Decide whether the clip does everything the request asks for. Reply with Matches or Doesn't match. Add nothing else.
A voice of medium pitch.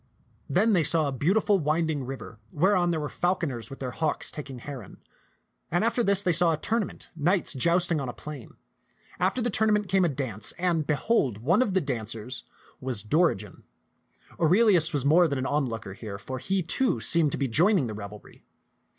Matches